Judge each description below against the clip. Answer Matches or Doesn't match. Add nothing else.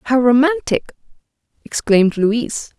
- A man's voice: Doesn't match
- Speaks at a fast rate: Doesn't match